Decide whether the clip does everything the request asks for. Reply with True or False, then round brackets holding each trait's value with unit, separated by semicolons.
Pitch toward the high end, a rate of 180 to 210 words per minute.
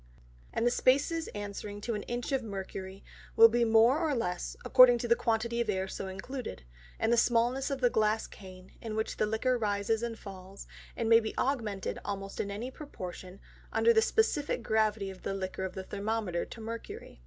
True (220 Hz; 200 wpm)